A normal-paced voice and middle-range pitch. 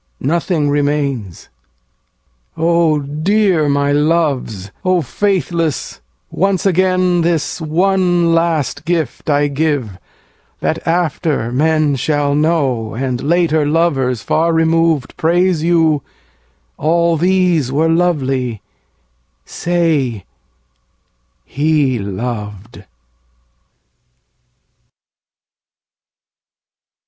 No: slow, 80 wpm; medium, 155 Hz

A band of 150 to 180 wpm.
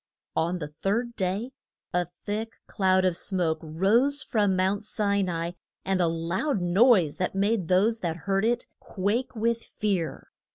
Yes: average, 160 wpm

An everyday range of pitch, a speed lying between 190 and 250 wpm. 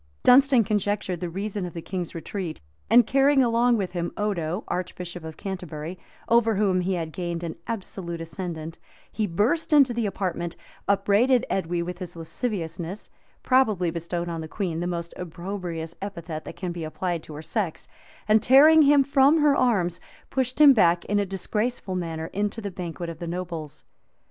No: average, 4.5 semitones; average, 175 wpm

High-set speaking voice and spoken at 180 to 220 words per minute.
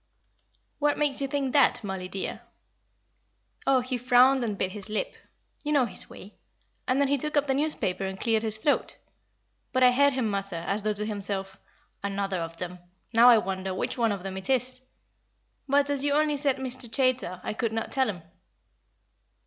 Yes: high, 235 Hz; average, 190 wpm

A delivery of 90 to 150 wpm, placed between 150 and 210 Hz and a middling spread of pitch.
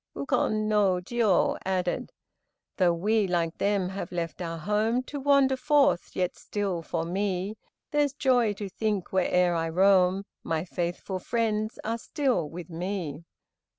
Yes: average, 145 wpm; high, 190 Hz; average, 3.7 semitones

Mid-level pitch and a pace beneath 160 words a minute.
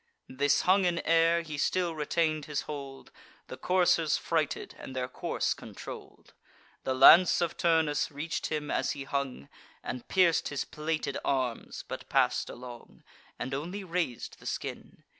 Yes: medium, 150 Hz; average, 150 wpm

